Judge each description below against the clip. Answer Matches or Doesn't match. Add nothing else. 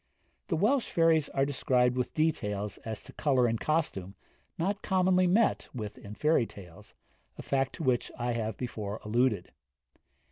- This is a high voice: Doesn't match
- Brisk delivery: Doesn't match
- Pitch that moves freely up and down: Matches